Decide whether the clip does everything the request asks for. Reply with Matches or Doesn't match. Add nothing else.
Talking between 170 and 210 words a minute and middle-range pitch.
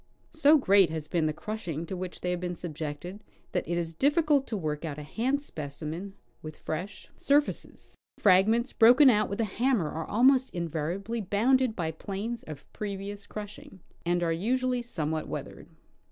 Doesn't match